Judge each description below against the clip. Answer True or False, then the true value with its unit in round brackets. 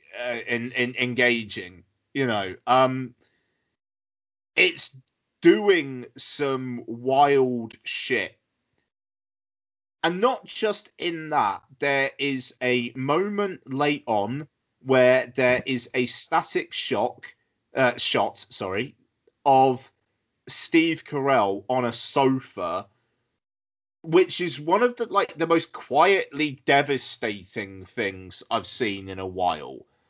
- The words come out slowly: True (110 wpm)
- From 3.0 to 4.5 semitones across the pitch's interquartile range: False (5.2 semitones)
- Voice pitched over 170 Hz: False (130 Hz)